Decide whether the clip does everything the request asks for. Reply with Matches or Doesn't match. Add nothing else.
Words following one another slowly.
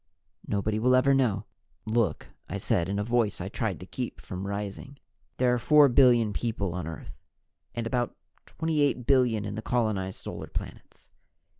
Doesn't match